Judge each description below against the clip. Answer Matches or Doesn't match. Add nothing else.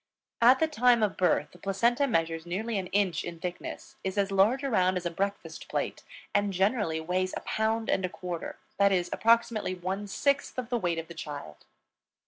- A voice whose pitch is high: Matches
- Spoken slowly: Doesn't match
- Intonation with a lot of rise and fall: Doesn't match